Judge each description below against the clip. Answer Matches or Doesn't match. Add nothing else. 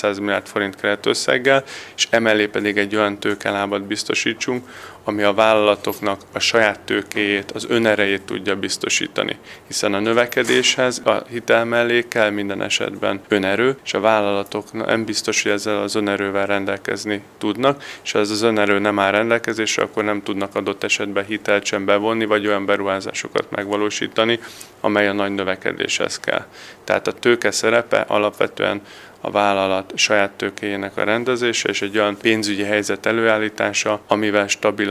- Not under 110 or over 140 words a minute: Doesn't match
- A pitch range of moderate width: Doesn't match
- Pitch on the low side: Matches